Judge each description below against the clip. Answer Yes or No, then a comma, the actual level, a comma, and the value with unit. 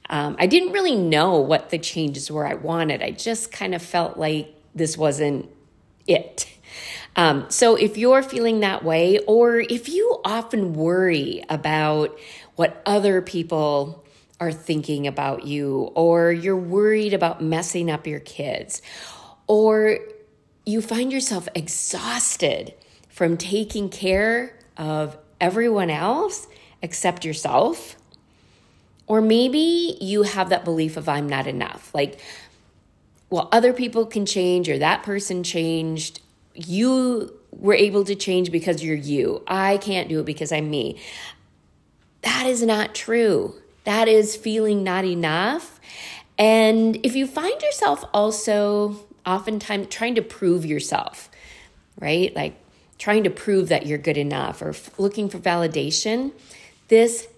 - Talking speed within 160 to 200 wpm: No, slow, 135 wpm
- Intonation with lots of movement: Yes, wide, 5.7 semitones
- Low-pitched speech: No, medium, 185 Hz